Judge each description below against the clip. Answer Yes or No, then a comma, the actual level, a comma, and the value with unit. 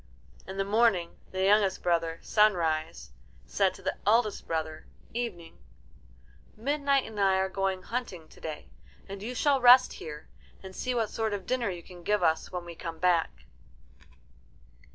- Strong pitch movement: No, average, 4.8 semitones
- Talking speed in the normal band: Yes, average, 160 wpm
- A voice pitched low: No, high, 195 Hz